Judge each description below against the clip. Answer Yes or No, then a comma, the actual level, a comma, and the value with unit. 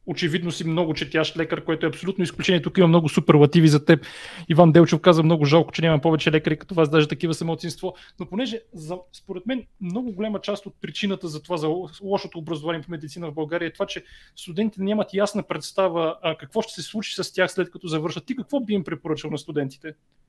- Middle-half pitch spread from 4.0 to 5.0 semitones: No, average, 2.8 semitones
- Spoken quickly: Yes, fast, 210 wpm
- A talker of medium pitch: Yes, medium, 170 Hz